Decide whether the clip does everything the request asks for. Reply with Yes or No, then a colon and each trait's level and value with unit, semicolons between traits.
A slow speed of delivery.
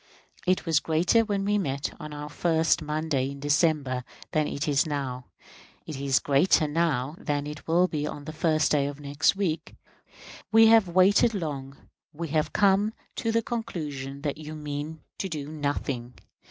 No: average, 170 wpm